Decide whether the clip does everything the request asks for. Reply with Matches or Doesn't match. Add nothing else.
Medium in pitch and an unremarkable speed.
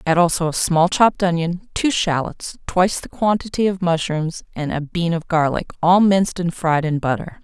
Matches